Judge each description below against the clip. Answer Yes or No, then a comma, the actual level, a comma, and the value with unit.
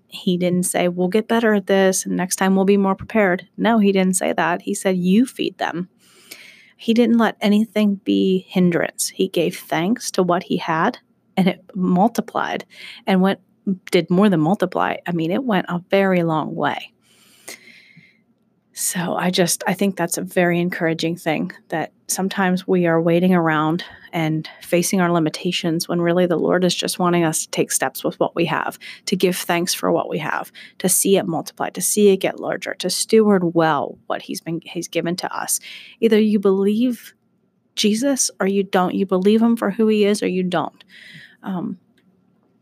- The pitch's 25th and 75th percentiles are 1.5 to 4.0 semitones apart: Yes, average, 2.7 semitones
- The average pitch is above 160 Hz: Yes, medium, 185 Hz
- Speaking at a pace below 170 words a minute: No, average, 190 wpm